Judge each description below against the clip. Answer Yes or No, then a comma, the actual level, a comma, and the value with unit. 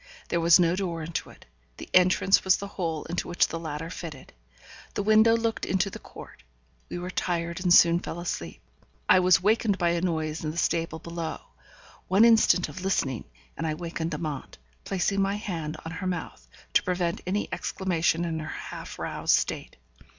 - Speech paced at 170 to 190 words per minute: Yes, average, 185 wpm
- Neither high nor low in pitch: Yes, medium, 175 Hz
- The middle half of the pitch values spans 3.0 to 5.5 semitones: No, narrow, 2.5 semitones